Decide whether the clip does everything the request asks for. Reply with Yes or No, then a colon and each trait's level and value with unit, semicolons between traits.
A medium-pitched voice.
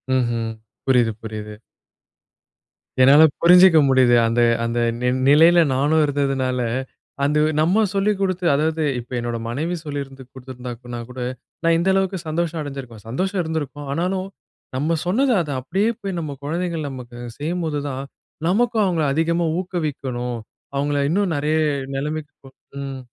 Yes: medium, 150 Hz